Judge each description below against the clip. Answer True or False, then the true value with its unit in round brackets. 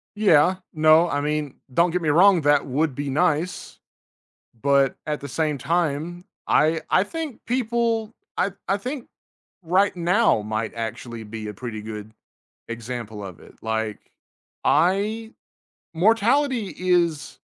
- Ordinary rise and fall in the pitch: False (7.5 semitones)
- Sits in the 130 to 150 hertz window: False (160 Hz)